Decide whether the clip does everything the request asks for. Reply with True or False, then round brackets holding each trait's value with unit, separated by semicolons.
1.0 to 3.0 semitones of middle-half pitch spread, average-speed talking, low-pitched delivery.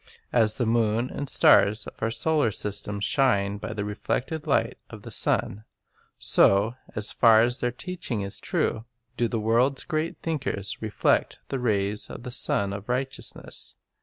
False (3.7 semitones; 165 wpm; 115 Hz)